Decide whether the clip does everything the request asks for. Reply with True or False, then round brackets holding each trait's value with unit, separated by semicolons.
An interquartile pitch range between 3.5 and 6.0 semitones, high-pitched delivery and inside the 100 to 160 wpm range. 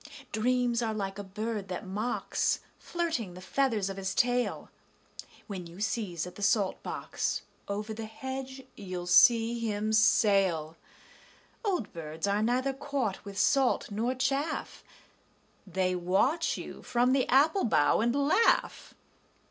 True (4.8 semitones; 220 Hz; 140 wpm)